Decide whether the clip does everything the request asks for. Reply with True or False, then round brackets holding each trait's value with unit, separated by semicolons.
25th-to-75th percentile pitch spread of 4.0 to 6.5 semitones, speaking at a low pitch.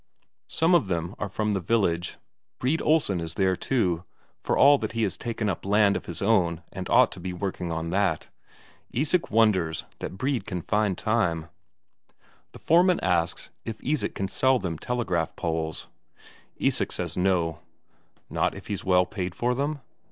True (5.2 semitones; 100 Hz)